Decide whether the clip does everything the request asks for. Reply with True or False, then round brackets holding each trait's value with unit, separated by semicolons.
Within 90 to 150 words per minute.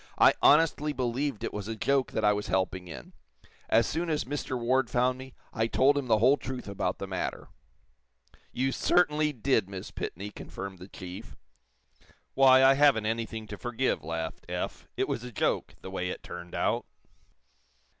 False (175 wpm)